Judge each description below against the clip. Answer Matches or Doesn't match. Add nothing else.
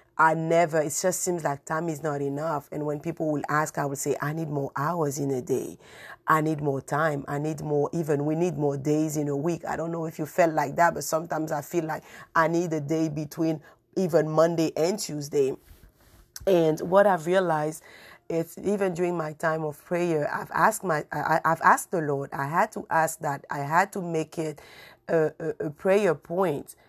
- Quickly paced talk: Matches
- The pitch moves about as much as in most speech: Doesn't match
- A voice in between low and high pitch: Matches